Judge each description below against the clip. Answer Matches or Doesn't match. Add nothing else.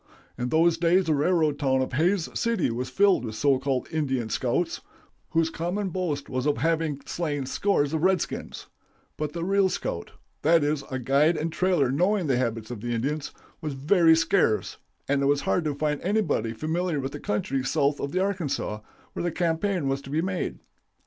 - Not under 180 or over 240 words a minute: Matches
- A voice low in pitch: Doesn't match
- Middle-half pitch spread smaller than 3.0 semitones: Doesn't match